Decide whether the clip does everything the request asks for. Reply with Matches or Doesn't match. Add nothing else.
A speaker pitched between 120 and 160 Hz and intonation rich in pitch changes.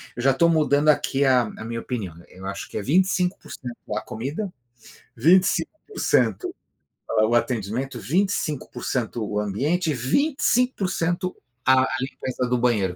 Matches